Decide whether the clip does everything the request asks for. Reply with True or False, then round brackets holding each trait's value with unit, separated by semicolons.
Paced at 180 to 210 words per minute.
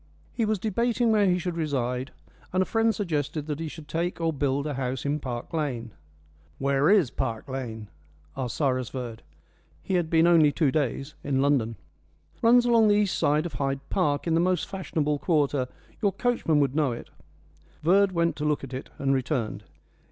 True (190 wpm)